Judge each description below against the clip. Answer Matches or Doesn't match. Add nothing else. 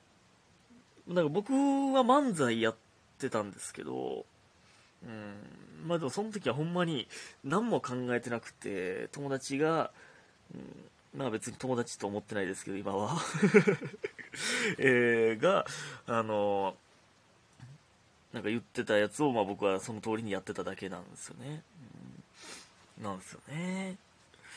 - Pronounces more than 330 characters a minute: Doesn't match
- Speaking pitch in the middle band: Doesn't match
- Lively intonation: Matches